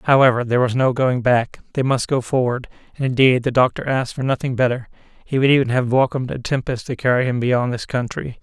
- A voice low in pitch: Yes, low, 125 Hz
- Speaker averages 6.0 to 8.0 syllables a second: Yes, 6.1 syllables/s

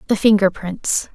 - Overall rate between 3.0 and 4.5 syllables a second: Yes, 4.4 syllables/s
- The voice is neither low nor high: No, high, 195 Hz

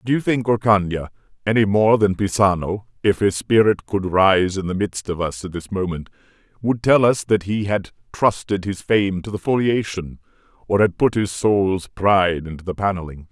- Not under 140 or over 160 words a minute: No, average, 190 wpm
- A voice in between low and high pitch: No, low, 100 Hz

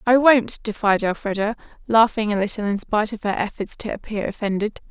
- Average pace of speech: Yes, average, 185 wpm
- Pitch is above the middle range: Yes, high, 215 Hz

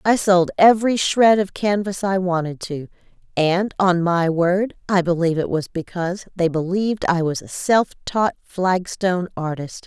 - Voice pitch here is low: No, medium, 180 Hz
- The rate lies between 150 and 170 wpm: Yes, average, 165 wpm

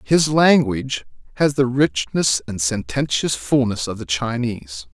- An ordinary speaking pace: No, slow, 130 wpm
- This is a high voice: No, low, 120 Hz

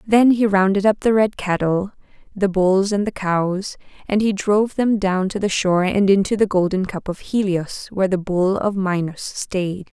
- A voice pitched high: Yes, high, 195 Hz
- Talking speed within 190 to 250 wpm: Yes, average, 200 wpm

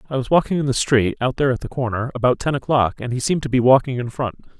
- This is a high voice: No, low, 130 Hz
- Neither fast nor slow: No, fast, 285 wpm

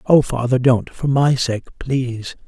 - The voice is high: No, low, 130 Hz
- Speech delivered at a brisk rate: No, average, 170 wpm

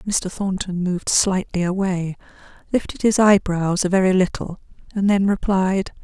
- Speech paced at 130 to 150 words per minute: Yes, average, 140 wpm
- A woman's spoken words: Yes, female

